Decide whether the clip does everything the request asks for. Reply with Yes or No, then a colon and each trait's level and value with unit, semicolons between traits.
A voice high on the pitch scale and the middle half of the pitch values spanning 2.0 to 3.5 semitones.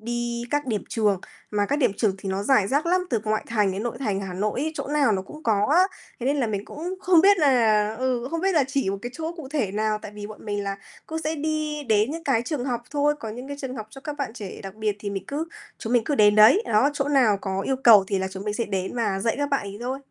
No: high, 235 Hz; wide, 5.6 semitones